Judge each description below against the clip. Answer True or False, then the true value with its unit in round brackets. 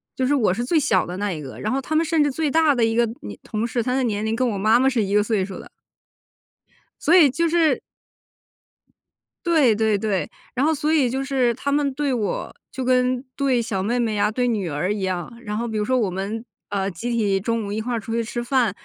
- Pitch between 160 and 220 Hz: False (235 Hz)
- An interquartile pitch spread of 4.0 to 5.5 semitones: True (4.3 semitones)